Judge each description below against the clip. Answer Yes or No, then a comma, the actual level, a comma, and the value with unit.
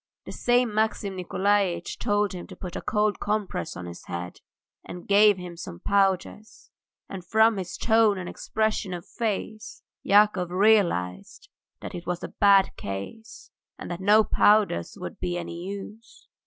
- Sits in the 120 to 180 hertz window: No, high, 195 Hz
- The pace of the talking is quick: No, average, 155 wpm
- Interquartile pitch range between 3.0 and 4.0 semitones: Yes, average, 3.3 semitones